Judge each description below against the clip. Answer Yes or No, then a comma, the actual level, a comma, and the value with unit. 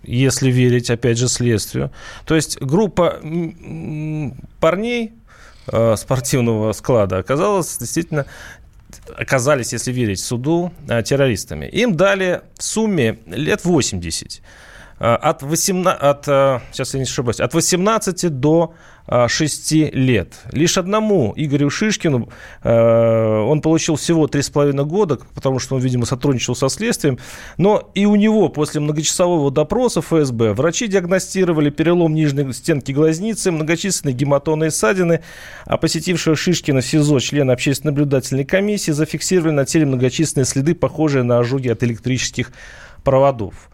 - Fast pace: No, average, 125 wpm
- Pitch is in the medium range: Yes, medium, 150 Hz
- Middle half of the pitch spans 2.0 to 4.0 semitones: No, average, 4.8 semitones